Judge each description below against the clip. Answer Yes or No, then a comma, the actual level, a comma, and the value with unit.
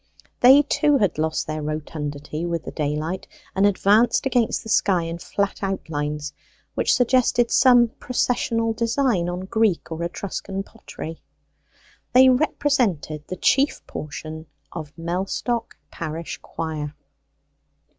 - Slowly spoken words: Yes, slow, 120 wpm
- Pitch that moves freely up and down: Yes, wide, 7.0 semitones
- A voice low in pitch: No, medium, 185 Hz